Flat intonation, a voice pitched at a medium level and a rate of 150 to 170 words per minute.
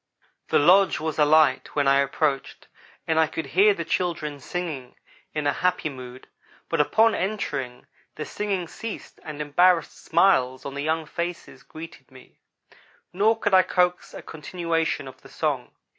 No: average, 4.1 semitones; medium, 160 Hz; average, 160 wpm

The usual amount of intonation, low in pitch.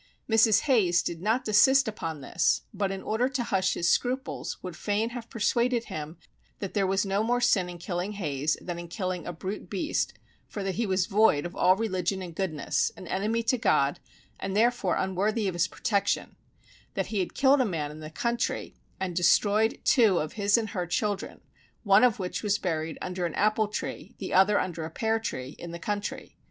No: average, 4.0 semitones; high, 195 Hz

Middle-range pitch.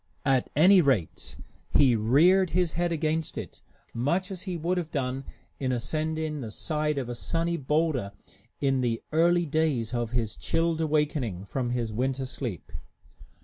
Yes: medium, 145 Hz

